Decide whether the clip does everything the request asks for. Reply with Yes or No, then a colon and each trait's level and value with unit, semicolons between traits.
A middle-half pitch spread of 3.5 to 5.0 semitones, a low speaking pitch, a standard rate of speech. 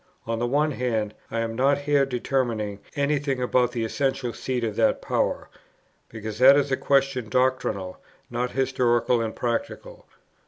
No: average, 2.9 semitones; low, 125 Hz; average, 165 wpm